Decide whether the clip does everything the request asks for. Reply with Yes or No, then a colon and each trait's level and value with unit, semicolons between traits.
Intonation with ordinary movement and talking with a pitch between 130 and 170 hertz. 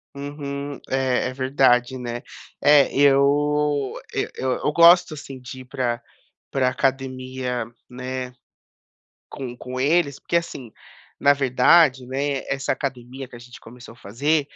No: narrow, 2.1 semitones; low, 135 Hz